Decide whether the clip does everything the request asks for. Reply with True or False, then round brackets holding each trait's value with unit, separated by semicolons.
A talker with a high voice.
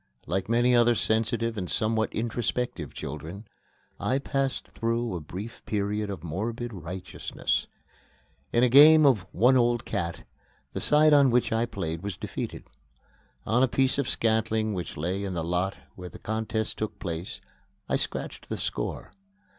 False (110 Hz)